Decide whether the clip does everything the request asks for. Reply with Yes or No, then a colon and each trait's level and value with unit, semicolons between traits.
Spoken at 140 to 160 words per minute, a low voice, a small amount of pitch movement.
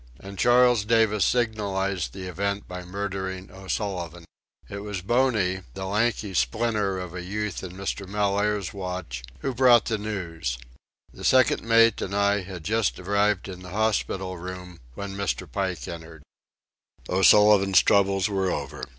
Yes: average, 145 wpm; low, 100 Hz; narrow, 2.3 semitones